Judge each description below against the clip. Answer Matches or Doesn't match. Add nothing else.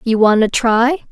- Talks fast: Matches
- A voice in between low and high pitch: Doesn't match